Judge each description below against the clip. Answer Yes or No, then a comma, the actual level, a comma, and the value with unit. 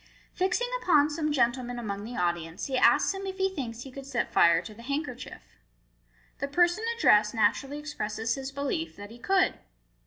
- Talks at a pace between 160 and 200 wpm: Yes, average, 180 wpm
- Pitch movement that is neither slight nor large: No, wide, 5.8 semitones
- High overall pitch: Yes, very high, 265 Hz